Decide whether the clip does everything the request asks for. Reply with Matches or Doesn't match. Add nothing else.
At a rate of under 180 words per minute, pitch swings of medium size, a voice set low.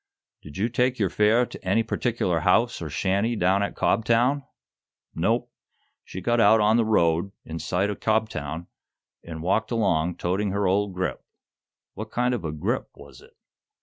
Matches